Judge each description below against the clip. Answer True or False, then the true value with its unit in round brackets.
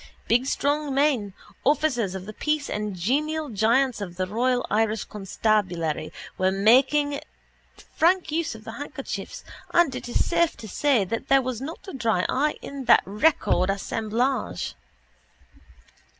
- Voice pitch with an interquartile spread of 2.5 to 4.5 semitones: False (5.6 semitones)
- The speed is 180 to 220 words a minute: False (145 wpm)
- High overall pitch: True (245 Hz)